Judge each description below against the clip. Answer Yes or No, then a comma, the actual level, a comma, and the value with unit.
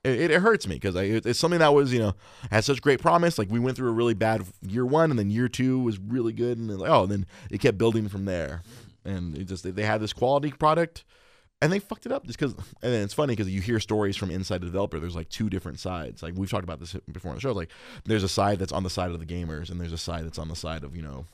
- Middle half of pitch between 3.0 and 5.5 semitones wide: Yes, average, 5.2 semitones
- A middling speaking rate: No, fast, 295 wpm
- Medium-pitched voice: No, low, 105 Hz